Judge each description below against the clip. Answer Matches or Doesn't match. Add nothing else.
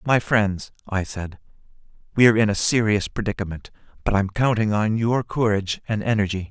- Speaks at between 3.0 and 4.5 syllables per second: Doesn't match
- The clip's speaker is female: Doesn't match